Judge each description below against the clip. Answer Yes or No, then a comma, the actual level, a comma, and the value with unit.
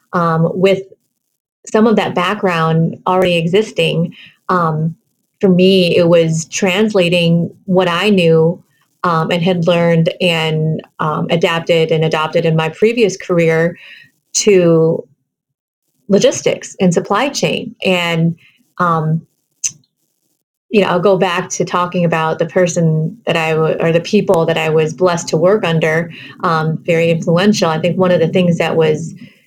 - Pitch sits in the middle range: Yes, medium, 175 Hz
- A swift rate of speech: No, average, 140 wpm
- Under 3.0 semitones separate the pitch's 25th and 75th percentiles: Yes, narrow, 2.4 semitones